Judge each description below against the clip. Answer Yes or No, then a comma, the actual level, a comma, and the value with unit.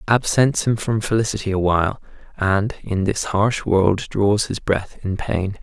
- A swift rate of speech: No, average, 170 wpm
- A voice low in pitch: Yes, low, 100 Hz